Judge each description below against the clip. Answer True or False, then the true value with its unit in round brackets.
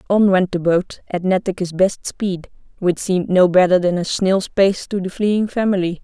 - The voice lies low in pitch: False (185 Hz)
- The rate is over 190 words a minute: True (200 wpm)